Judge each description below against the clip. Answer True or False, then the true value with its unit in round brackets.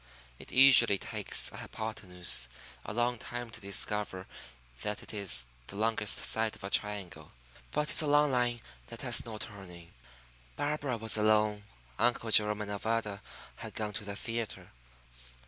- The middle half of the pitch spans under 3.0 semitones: True (2.6 semitones)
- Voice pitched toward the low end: True (110 Hz)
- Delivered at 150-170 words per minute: True (155 wpm)